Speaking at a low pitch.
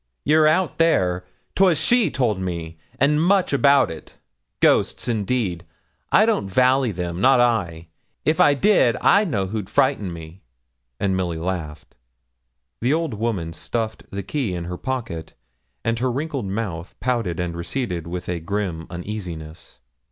Yes: low, 105 Hz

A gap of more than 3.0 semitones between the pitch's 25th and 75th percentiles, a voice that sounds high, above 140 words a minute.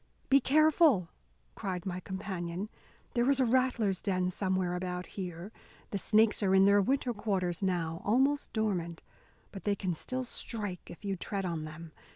Yes: average, 3.9 semitones; high, 195 Hz; average, 165 wpm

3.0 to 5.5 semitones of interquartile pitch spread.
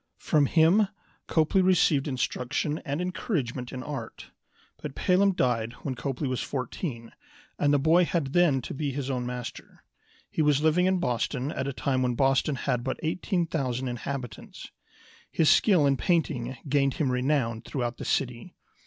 Yes: average, 3.9 semitones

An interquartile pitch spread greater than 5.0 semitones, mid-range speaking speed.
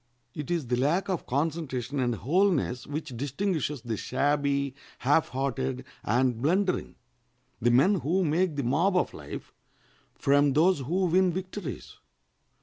No: wide, 5.5 semitones; slow, 130 wpm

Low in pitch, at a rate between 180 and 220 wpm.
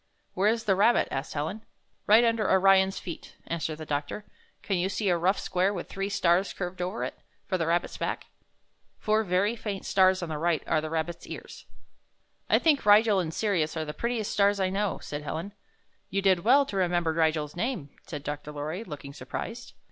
No: medium, 185 Hz; average, 195 wpm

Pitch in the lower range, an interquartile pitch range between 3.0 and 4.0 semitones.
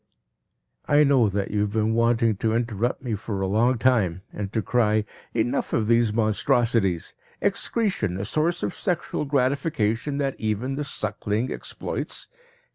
Yes: low, 115 Hz; average, 3.6 semitones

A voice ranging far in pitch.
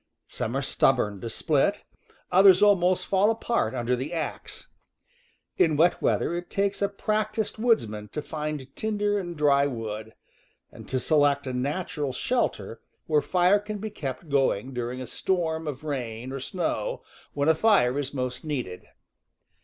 Yes: wide, 6.9 semitones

